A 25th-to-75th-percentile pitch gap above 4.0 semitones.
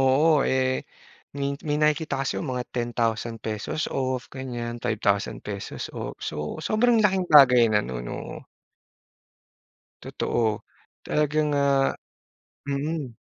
Yes: average, 4.4 semitones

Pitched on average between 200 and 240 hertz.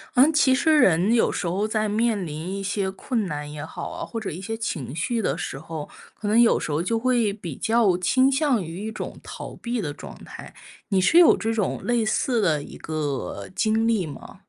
Yes: high, 205 Hz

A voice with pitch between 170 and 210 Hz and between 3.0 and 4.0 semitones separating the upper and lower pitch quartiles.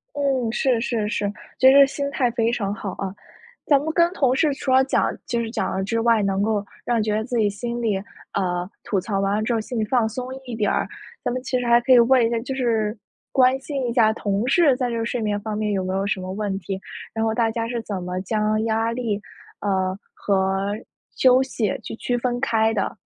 No: high, 225 Hz; average, 3.4 semitones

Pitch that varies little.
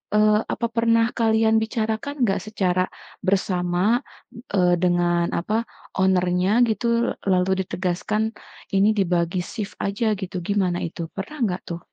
No: average, 3.6 semitones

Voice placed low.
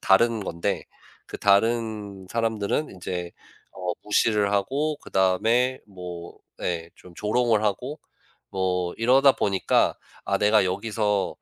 Yes: low, 105 Hz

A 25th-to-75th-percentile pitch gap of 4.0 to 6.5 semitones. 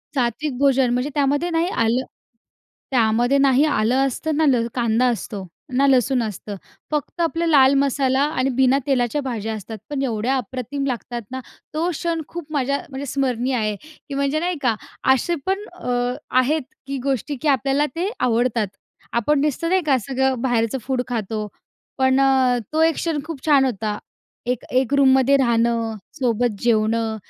No: average, 3.2 semitones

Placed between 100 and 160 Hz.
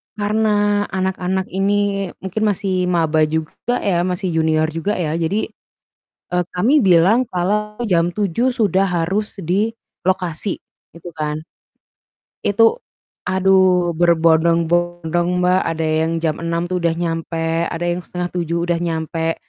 No: medium, 180 Hz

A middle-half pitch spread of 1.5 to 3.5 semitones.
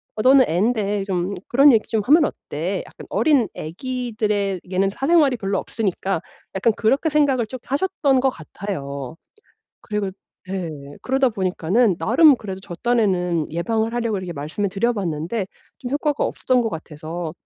No: wide, 5.6 semitones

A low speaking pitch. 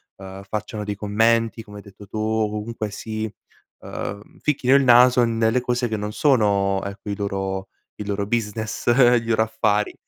Yes: low, 110 Hz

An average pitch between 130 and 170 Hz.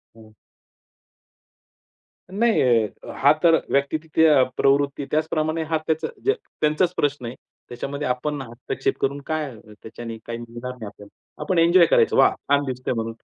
Yes: medium, 140 Hz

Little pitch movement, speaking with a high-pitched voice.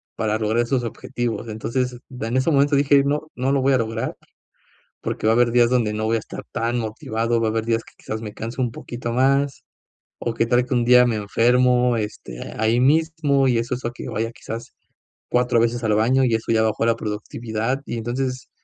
No: narrow, 2.1 semitones; low, 120 Hz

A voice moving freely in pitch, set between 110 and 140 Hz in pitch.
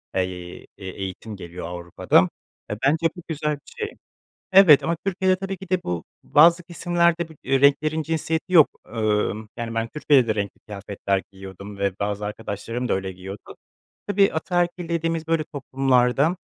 Yes: wide, 8.6 semitones; low, 135 Hz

